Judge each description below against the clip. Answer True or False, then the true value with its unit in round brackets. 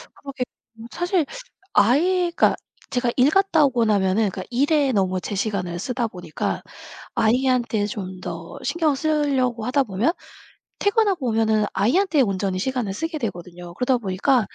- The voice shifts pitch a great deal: True (6.3 semitones)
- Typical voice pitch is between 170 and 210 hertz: False (240 Hz)